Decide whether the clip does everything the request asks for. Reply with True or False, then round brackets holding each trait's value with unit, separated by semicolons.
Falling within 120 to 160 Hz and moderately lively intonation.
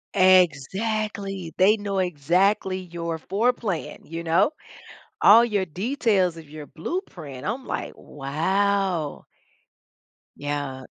False (185 Hz; 4.3 semitones)